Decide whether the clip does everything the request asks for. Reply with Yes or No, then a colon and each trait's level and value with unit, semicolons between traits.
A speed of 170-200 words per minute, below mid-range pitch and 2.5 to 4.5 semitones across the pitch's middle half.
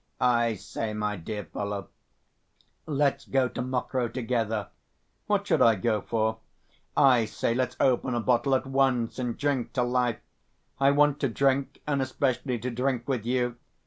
No: average, 160 wpm; low, 125 Hz; average, 2.8 semitones